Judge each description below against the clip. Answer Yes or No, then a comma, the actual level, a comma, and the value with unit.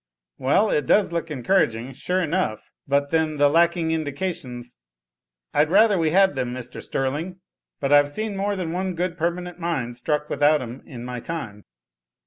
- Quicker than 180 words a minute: No, average, 170 wpm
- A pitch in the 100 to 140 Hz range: No, medium, 155 Hz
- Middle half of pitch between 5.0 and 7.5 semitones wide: Yes, wide, 5.6 semitones